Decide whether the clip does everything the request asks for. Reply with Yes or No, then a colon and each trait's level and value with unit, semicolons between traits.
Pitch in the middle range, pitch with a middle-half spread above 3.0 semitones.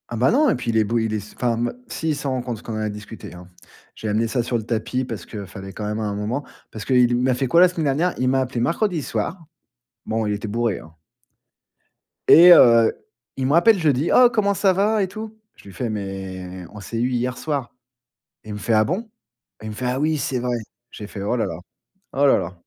No: low, 120 Hz; wide, 5.4 semitones